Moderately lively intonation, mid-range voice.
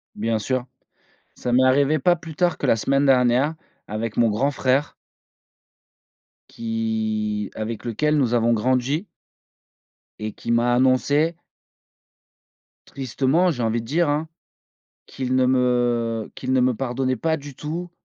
No: average, 3.7 semitones; low, 130 Hz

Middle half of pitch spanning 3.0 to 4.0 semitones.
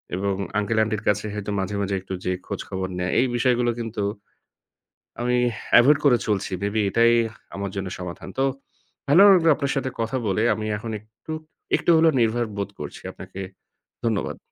Yes: average, 3.4 semitones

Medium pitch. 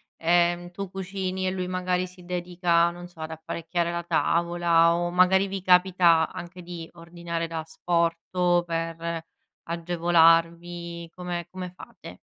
Yes: medium, 175 Hz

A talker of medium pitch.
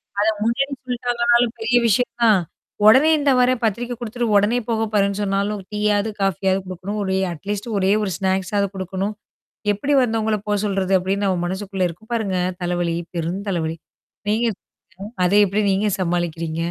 No: high, 200 Hz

